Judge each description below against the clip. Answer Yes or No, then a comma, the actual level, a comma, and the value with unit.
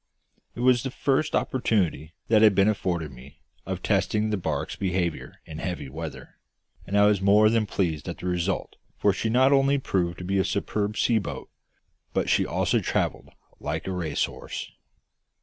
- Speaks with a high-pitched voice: No, low, 100 Hz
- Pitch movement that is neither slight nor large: Yes, average, 4.2 semitones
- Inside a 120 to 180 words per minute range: Yes, average, 175 wpm